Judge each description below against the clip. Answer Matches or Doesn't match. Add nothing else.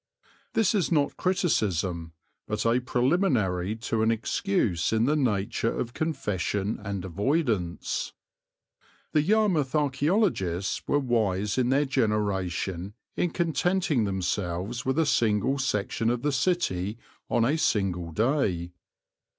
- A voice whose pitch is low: Matches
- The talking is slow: Matches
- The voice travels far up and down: Matches